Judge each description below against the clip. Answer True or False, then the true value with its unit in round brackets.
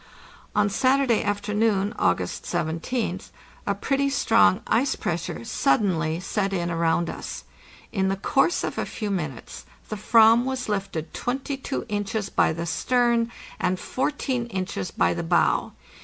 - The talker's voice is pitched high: True (205 Hz)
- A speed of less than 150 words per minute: True (140 wpm)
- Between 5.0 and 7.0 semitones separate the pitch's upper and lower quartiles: True (5.6 semitones)